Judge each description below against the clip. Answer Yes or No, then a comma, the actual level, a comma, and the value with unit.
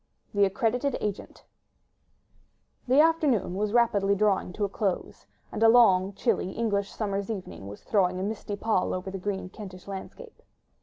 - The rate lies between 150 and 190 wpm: Yes, average, 155 wpm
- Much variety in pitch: No, average, 2.9 semitones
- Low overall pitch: No, high, 200 Hz